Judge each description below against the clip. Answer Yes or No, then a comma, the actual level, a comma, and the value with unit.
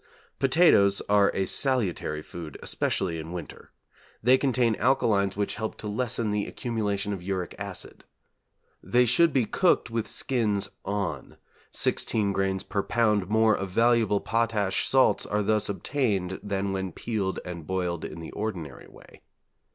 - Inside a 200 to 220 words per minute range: No, average, 145 wpm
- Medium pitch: No, low, 105 Hz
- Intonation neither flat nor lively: Yes, average, 3.3 semitones